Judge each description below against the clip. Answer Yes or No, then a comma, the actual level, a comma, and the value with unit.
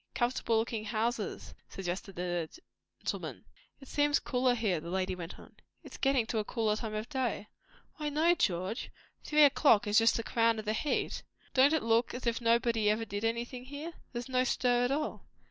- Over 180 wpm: Yes, average, 195 wpm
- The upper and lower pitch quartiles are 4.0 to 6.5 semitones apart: No, average, 3.4 semitones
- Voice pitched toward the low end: No, high, 230 Hz